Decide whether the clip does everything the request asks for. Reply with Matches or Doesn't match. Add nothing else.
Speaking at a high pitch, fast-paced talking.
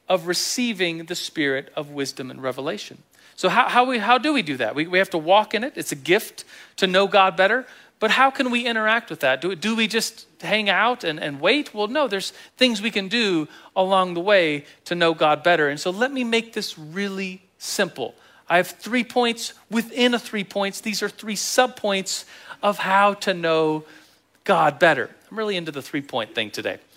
Matches